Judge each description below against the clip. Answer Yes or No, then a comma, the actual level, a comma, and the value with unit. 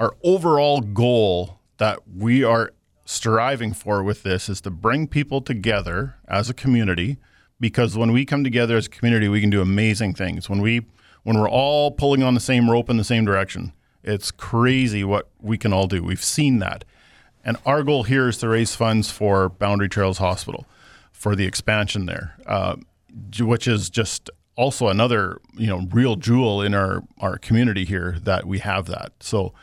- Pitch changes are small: No, average, 3.9 semitones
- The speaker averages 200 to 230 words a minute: No, average, 185 wpm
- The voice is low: Yes, low, 110 Hz